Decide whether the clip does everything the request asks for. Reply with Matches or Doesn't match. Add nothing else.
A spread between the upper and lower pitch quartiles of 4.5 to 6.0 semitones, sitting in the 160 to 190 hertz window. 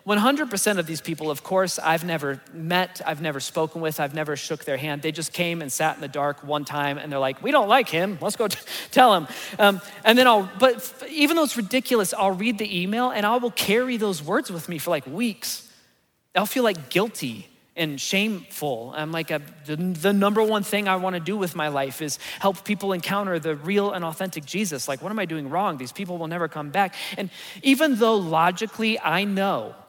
Matches